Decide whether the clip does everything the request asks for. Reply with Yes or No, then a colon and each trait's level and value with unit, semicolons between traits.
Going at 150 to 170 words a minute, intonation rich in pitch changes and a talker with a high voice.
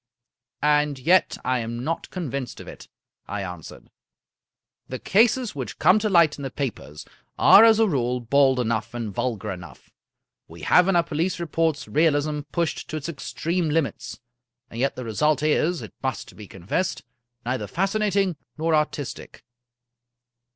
No: average, 160 wpm; wide, 5.7 semitones; medium, 150 Hz